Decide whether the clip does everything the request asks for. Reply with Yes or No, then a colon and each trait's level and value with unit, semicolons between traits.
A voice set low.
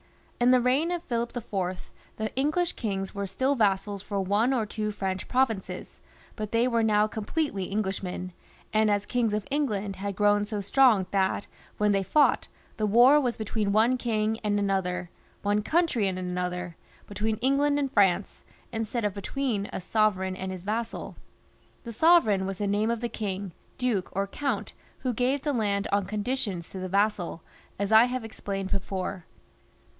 No: high, 210 Hz